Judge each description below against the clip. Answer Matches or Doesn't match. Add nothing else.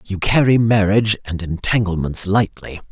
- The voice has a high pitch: Doesn't match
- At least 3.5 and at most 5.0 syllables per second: Matches